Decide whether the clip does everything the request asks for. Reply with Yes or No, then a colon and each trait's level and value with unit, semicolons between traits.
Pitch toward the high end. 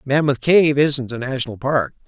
No: low, 130 Hz